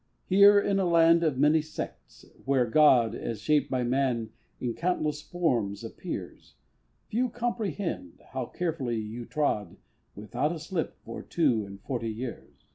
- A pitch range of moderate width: No, wide, 6.3 semitones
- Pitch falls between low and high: Yes, medium, 145 Hz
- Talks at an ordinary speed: Yes, average, 145 wpm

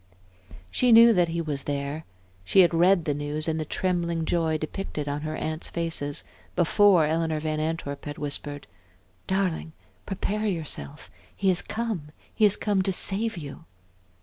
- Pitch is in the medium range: Yes, medium, 165 Hz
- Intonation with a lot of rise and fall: No, average, 3.9 semitones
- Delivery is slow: No, average, 160 wpm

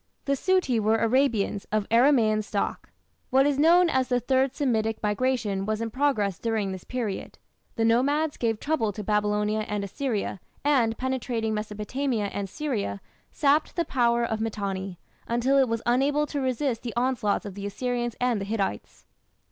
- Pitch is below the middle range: No, high, 230 Hz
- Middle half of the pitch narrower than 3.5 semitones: No, average, 3.9 semitones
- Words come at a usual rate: Yes, average, 165 wpm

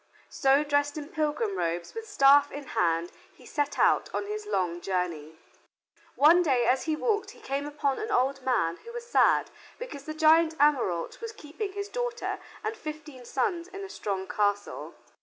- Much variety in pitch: Yes, wide, 7.9 semitones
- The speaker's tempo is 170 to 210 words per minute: Yes, average, 175 wpm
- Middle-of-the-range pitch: No, very high, 295 Hz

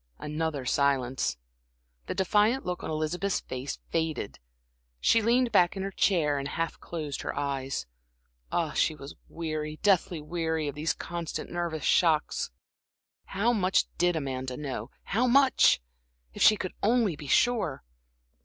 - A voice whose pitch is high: No, medium, 160 Hz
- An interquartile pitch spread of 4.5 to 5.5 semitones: Yes, average, 4.8 semitones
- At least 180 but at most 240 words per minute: No, average, 145 wpm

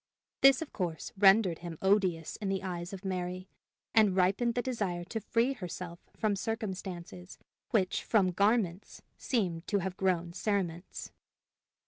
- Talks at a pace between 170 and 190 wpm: No, average, 140 wpm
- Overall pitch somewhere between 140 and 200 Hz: Yes, high, 190 Hz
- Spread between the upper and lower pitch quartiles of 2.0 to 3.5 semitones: Yes, average, 3.2 semitones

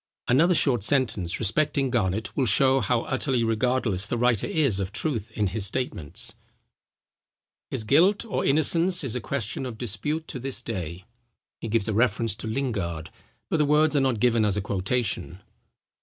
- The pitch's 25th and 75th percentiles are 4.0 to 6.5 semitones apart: Yes, average, 4.8 semitones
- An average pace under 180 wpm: Yes, average, 170 wpm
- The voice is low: Yes, low, 120 Hz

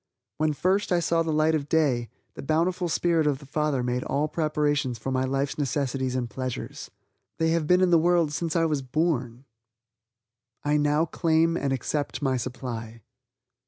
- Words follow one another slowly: No, average, 175 wpm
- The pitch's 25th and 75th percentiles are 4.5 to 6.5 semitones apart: No, average, 3.8 semitones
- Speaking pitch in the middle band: Yes, medium, 150 Hz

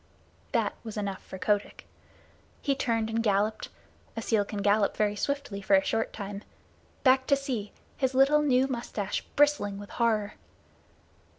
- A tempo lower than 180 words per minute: Yes, average, 160 wpm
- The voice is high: Yes, high, 220 Hz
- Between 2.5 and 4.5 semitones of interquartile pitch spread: Yes, average, 4.2 semitones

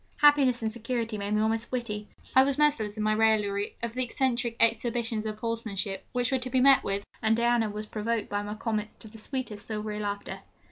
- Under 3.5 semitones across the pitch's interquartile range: Yes, narrow, 2.4 semitones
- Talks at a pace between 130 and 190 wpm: No, fast, 205 wpm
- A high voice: Yes, high, 225 Hz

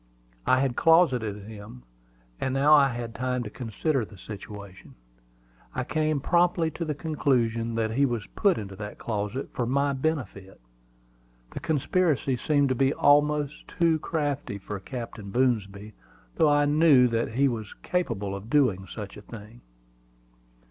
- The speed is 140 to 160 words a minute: Yes, average, 150 wpm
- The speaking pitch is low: Yes, low, 125 Hz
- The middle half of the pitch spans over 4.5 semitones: Yes, wide, 5.5 semitones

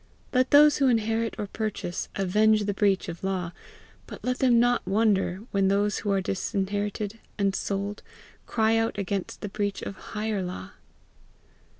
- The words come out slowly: No, average, 160 wpm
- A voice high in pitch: Yes, high, 205 Hz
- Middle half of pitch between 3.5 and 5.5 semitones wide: No, narrow, 2.4 semitones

